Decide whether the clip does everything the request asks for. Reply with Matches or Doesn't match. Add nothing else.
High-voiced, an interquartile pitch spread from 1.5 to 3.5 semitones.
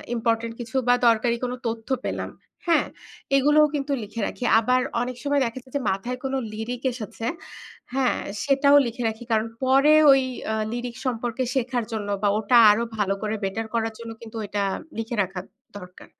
Matches